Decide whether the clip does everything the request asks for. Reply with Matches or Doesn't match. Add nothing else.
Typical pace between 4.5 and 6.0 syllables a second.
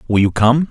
Matches